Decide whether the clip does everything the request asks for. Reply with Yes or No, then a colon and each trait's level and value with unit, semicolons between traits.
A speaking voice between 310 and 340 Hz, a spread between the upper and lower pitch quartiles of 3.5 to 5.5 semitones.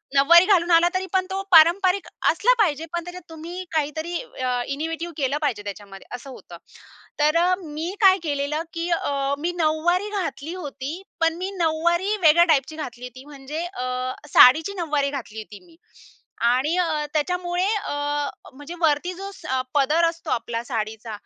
Yes: very high, 315 Hz; average, 3.9 semitones